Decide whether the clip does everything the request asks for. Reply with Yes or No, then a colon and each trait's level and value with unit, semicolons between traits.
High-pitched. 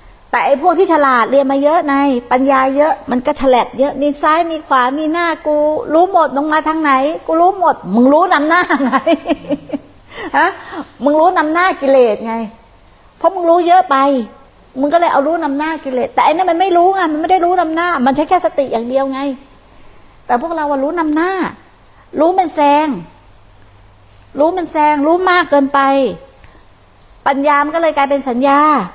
Yes: very high, 295 Hz